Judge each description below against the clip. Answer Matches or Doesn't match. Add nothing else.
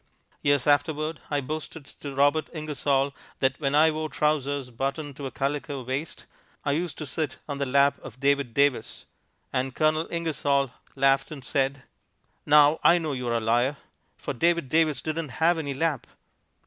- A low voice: Doesn't match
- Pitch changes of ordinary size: Doesn't match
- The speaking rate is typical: Matches